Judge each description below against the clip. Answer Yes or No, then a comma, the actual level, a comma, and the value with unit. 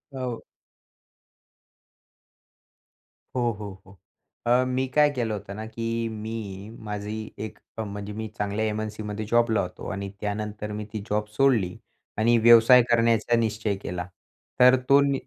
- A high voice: No, low, 110 Hz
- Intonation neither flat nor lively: No, narrow, 2.2 semitones